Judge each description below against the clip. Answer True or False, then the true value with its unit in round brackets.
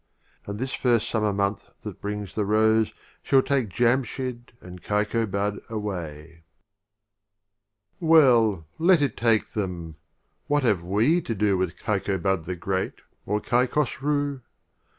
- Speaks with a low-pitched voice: True (105 Hz)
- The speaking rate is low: True (130 wpm)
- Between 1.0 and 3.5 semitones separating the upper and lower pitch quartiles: False (4.5 semitones)